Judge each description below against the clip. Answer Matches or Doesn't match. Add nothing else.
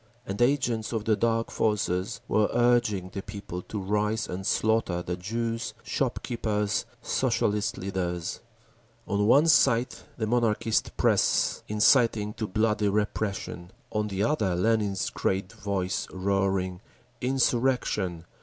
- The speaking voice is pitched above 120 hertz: Doesn't match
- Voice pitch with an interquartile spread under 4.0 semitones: Matches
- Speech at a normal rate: Doesn't match